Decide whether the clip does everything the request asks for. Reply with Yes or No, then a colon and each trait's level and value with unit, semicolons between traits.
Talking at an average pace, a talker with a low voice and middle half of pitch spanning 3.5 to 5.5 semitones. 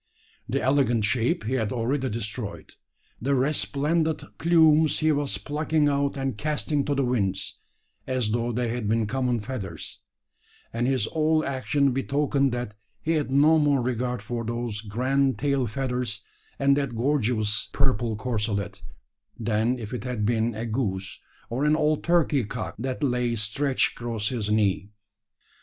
Yes: average, 150 wpm; low, 125 Hz; average, 3.9 semitones